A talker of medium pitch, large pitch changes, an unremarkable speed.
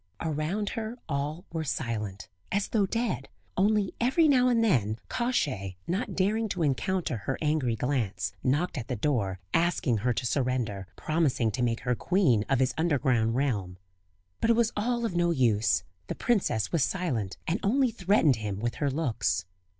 Yes: medium, 145 Hz; wide, 9.0 semitones; average, 170 wpm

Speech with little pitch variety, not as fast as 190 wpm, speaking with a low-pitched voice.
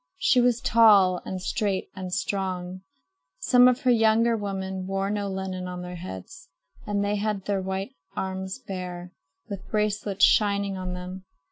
No: narrow, 2.1 semitones; average, 150 wpm; high, 195 Hz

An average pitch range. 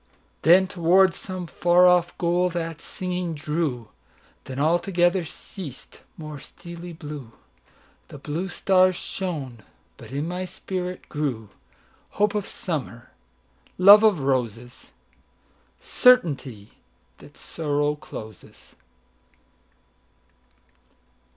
Yes: average, 4.4 semitones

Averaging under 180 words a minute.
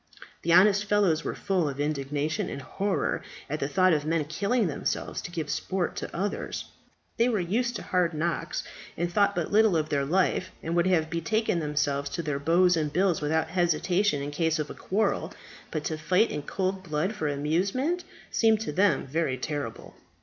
No: average, 190 wpm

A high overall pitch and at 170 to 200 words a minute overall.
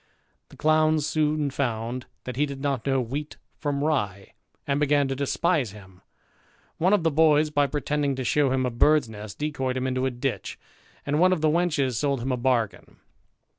No: medium, 140 Hz; average, 190 wpm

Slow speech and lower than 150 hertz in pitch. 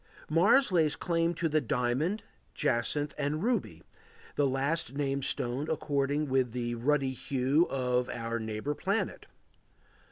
Yes: slow, 130 wpm; medium, 140 Hz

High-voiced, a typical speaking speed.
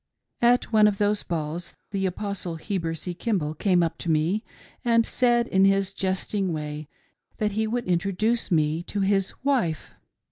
Yes: high, 195 Hz; average, 165 wpm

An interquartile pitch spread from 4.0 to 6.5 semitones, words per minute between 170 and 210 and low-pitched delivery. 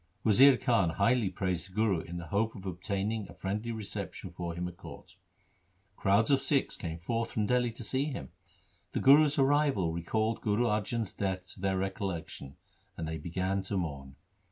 Yes: average, 4.7 semitones; average, 180 wpm; low, 100 Hz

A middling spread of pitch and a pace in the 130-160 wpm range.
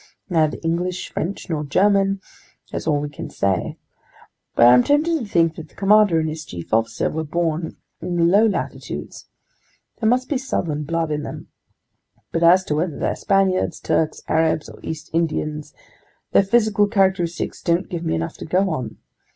No: average, 4.0 semitones; average, 175 wpm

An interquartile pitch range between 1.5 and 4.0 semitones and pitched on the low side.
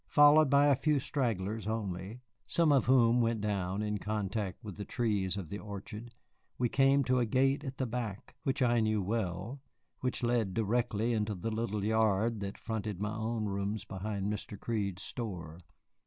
Yes: average, 3.3 semitones; low, 110 Hz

